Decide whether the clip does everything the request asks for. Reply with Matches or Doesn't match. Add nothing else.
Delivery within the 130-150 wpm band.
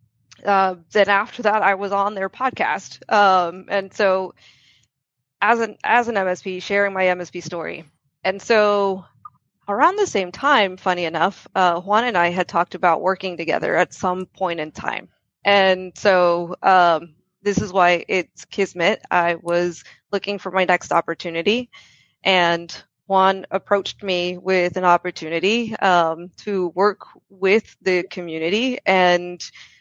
Matches